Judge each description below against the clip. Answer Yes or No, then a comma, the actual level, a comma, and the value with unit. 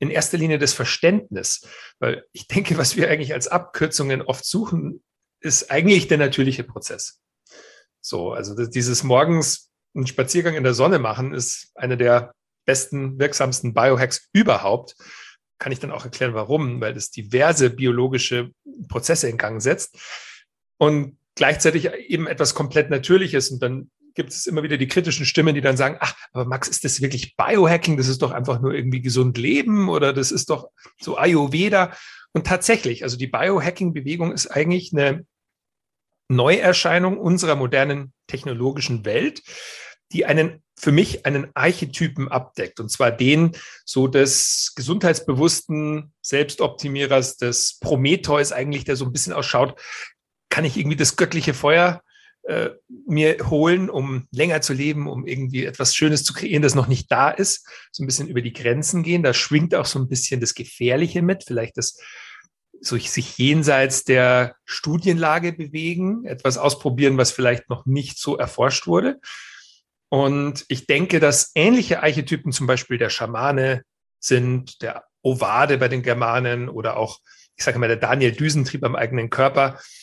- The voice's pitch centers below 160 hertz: Yes, medium, 140 Hz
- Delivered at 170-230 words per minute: No, average, 155 wpm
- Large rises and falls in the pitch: No, average, 4.0 semitones